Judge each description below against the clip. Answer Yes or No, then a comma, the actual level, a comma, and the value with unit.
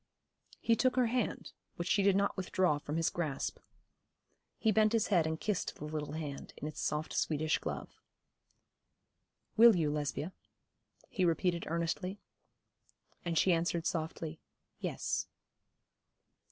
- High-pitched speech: No, medium, 170 Hz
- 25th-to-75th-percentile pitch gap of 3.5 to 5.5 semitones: Yes, average, 4.2 semitones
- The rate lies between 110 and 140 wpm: Yes, slow, 135 wpm